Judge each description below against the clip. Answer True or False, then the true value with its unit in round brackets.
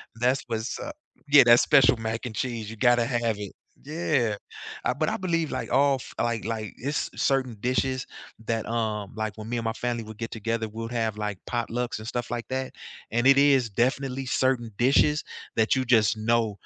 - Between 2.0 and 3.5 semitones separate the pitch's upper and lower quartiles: True (2.7 semitones)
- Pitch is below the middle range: True (120 Hz)